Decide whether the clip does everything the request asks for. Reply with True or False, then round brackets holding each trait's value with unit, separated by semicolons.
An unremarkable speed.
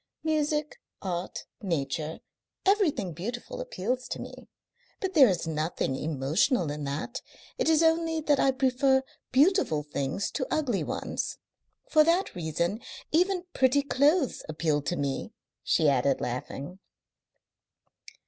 False (125 wpm)